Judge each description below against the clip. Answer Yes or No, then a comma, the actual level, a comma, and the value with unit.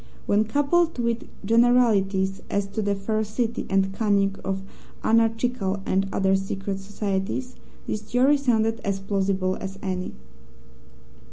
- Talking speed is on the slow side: Yes, slow, 120 wpm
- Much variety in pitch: No, average, 3.0 semitones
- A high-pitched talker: Yes, high, 205 Hz